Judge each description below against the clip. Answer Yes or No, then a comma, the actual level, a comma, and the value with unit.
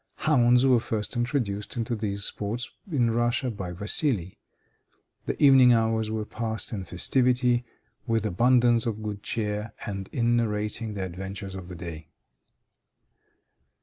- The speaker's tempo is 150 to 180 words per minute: No, slow, 135 wpm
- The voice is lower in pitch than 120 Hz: Yes, low, 110 Hz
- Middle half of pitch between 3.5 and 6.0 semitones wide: No, average, 3.1 semitones